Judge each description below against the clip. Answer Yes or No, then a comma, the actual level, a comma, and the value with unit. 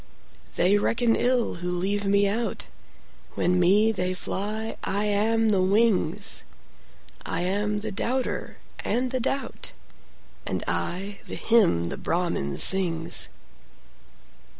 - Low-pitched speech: No, high, 205 Hz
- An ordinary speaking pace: No, slow, 105 wpm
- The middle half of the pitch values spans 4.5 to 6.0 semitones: No, average, 3.6 semitones